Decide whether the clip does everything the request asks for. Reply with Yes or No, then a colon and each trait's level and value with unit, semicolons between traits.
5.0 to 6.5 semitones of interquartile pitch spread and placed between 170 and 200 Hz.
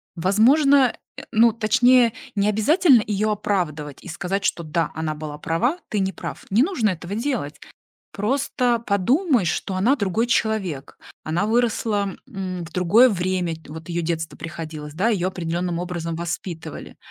Yes: average, 5.3 semitones; high, 190 Hz